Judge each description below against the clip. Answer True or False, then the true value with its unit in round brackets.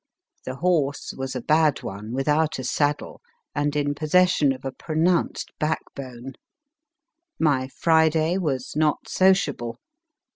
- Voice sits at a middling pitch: True (145 Hz)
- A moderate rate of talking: False (120 wpm)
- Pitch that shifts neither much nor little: True (3.2 semitones)